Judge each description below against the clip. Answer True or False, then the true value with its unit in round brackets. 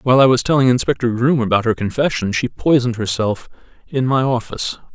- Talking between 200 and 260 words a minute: False (180 wpm)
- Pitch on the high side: False (120 Hz)